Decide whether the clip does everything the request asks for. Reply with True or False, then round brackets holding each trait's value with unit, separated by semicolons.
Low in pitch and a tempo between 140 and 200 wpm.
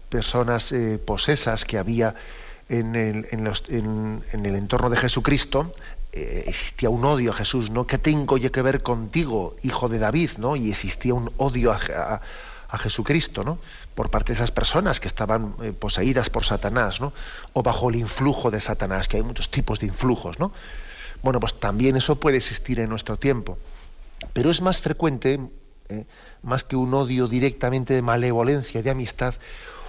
True (120 Hz; 180 wpm)